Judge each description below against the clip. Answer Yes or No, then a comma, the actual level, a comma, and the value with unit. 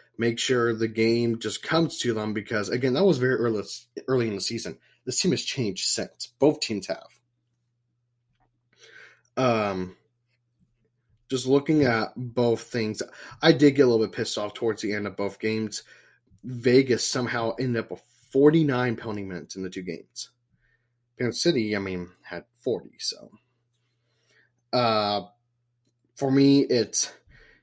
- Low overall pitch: Yes, low, 120 Hz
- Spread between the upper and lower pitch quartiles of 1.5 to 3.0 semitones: Yes, narrow, 2.4 semitones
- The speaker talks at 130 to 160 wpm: Yes, average, 150 wpm